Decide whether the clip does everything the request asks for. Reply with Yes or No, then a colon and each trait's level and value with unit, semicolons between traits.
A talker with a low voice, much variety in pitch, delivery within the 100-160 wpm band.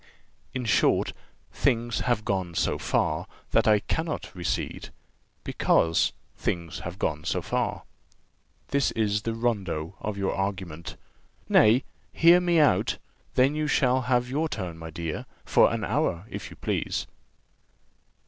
Yes: low, 110 Hz; wide, 6.4 semitones; average, 140 wpm